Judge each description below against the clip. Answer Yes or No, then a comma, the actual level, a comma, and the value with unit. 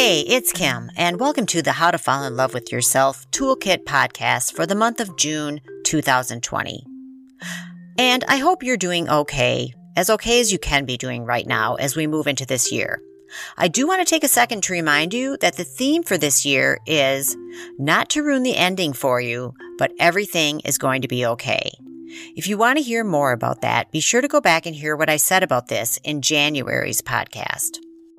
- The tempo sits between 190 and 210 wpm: Yes, fast, 205 wpm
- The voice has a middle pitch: Yes, medium, 155 Hz